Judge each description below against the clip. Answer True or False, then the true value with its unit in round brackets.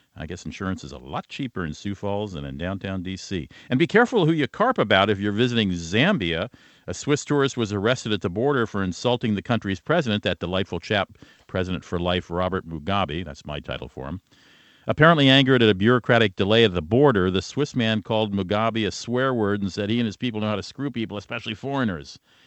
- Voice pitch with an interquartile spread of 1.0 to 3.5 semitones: False (4.5 semitones)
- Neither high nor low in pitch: False (105 Hz)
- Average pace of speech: False (215 wpm)